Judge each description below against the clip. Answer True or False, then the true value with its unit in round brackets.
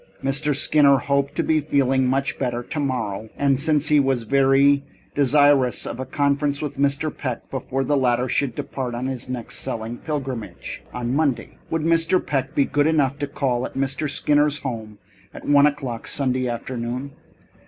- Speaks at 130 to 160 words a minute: False (170 wpm)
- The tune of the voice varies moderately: False (2.3 semitones)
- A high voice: False (135 Hz)